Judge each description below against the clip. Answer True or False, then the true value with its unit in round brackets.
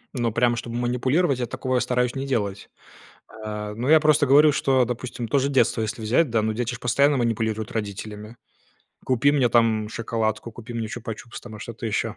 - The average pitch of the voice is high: False (120 Hz)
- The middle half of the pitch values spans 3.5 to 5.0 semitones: False (2.8 semitones)